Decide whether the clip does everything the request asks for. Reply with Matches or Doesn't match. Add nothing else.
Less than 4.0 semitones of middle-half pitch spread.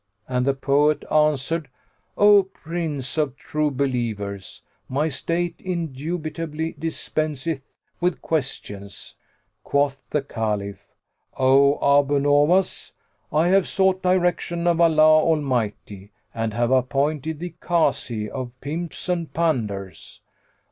Doesn't match